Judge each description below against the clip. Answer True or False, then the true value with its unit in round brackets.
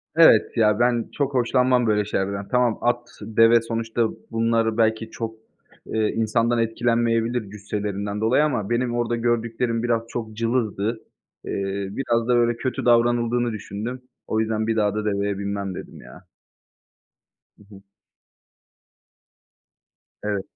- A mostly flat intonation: True (2.0 semitones)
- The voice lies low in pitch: True (115 Hz)